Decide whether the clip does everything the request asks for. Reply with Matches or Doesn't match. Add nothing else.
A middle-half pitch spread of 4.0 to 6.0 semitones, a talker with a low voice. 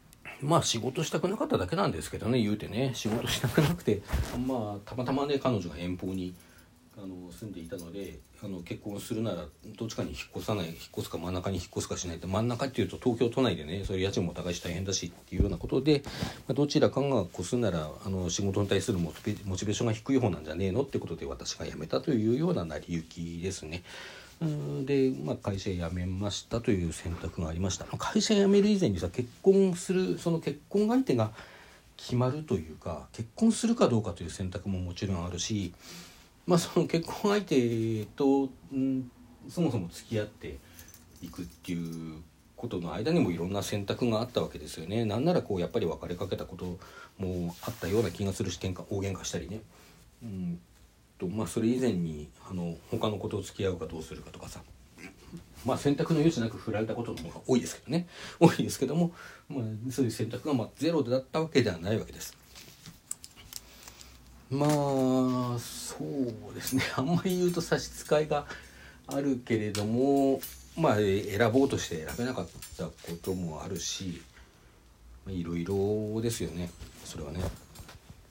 Doesn't match